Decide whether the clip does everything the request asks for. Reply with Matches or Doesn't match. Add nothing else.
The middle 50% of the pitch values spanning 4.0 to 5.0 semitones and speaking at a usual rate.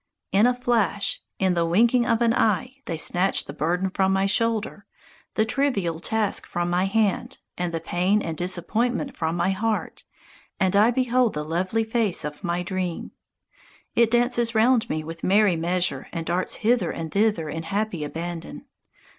Matches